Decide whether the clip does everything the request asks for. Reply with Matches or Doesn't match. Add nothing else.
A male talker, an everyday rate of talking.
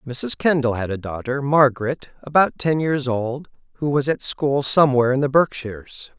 Matches